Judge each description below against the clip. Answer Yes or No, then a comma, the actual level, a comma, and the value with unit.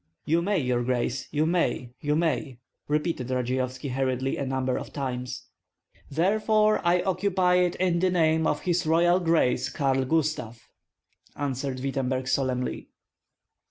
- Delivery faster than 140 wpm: No, slow, 135 wpm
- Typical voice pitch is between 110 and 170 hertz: Yes, medium, 140 Hz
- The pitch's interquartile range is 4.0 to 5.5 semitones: Yes, average, 5.0 semitones